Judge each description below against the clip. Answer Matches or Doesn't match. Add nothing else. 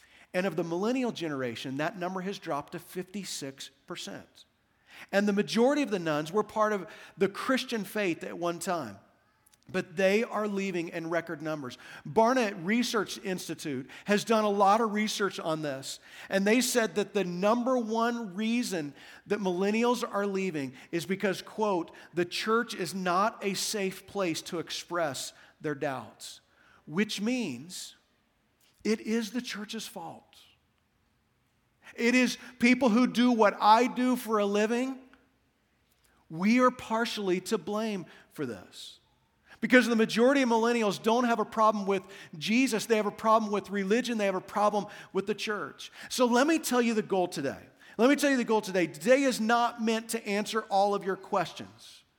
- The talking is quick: Doesn't match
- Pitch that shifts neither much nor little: Matches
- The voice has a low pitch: Doesn't match